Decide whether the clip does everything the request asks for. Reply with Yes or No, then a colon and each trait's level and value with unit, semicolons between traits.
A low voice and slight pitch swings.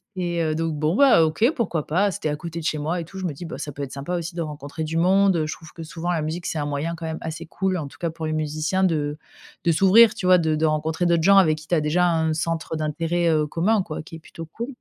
No: medium, 165 Hz; narrow, 2.2 semitones